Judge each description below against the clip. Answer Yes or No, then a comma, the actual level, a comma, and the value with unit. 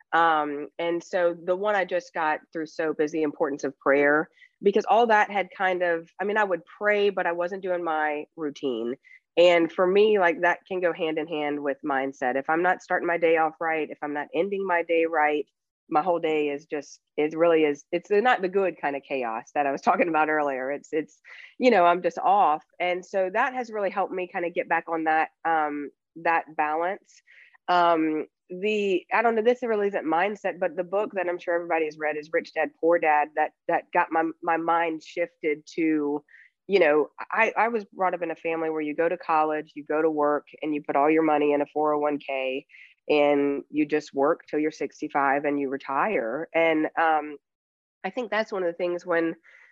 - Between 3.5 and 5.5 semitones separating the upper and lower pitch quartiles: No, average, 3.1 semitones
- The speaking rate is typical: No, fast, 225 wpm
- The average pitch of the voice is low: No, medium, 165 Hz